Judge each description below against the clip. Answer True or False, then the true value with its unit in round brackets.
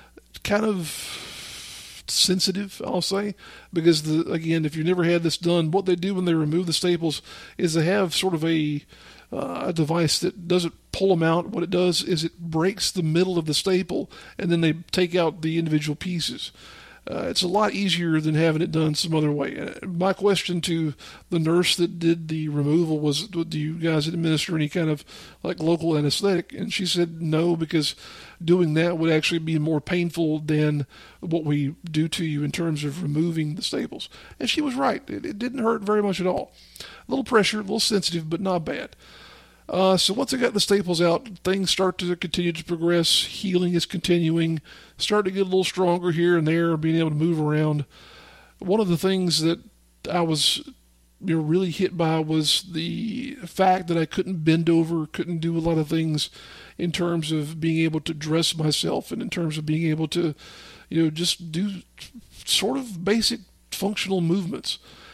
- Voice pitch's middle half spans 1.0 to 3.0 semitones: True (2.5 semitones)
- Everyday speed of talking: True (195 wpm)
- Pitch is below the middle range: False (170 Hz)